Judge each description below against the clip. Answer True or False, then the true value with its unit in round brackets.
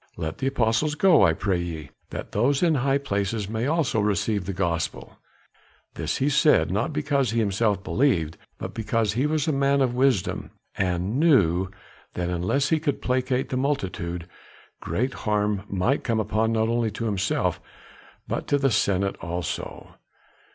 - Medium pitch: False (110 Hz)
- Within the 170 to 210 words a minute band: False (160 wpm)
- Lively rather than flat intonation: True (6.1 semitones)